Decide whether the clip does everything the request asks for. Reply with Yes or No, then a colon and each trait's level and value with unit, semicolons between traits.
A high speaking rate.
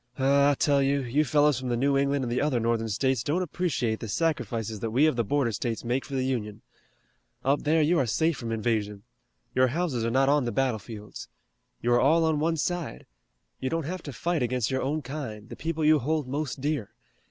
Yes: fast, 220 wpm